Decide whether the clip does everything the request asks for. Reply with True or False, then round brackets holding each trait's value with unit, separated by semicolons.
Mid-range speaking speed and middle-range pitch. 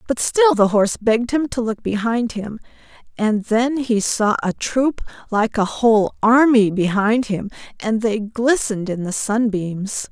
False (165 wpm; 225 Hz)